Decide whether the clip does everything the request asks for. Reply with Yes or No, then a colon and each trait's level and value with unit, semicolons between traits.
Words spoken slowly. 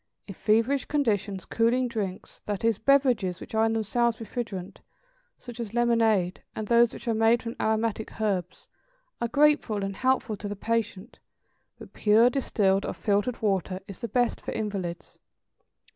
No: average, 160 wpm